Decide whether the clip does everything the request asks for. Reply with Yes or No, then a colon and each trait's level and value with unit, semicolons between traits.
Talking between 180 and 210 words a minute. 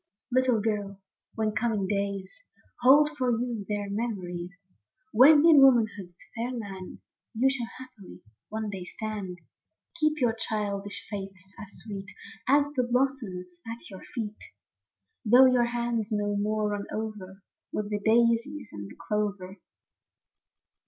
No: slow, 135 wpm